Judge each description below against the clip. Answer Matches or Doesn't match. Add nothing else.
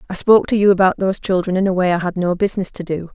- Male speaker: Doesn't match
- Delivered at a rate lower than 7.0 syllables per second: Doesn't match